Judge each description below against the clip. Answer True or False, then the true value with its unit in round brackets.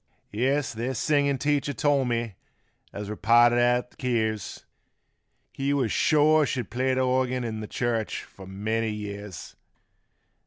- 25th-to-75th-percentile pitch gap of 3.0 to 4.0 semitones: True (3.5 semitones)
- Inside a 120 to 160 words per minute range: True (145 wpm)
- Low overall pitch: True (120 Hz)